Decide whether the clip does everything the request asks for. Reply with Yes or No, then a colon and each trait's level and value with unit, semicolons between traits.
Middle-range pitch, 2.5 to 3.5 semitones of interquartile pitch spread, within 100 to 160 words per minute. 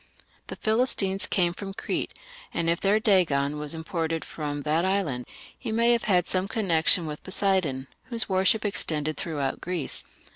No: medium, 180 Hz; average, 4.4 semitones; average, 155 wpm